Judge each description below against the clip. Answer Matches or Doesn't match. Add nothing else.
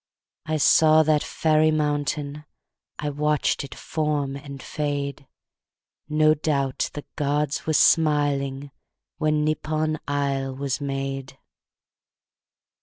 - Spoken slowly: Matches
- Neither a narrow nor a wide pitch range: Doesn't match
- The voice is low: Doesn't match